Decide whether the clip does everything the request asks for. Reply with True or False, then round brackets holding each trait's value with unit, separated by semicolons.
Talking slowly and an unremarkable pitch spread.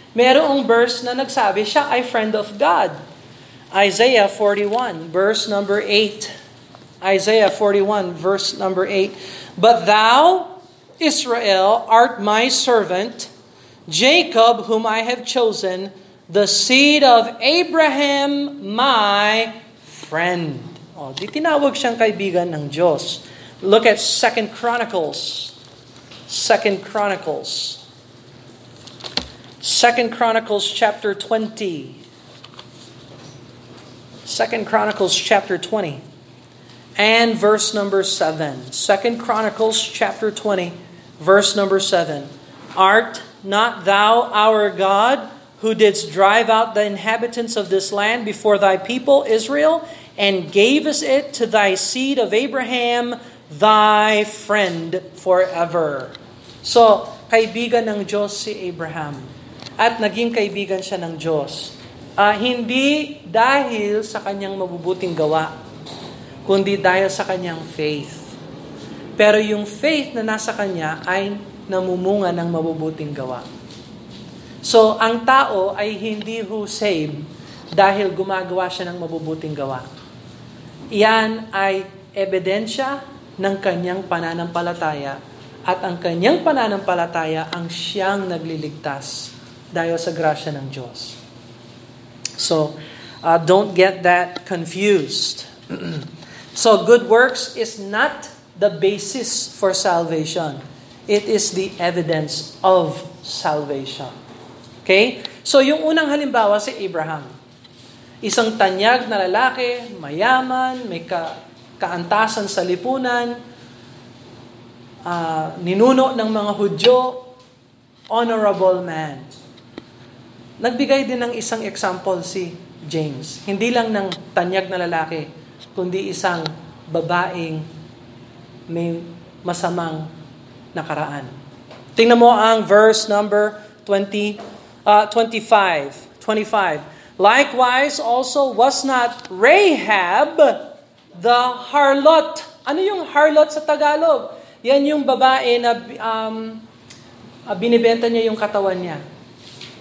False (105 wpm; 6.1 semitones)